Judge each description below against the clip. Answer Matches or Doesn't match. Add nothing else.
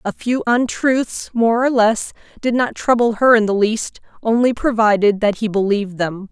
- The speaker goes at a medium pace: Matches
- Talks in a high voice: Matches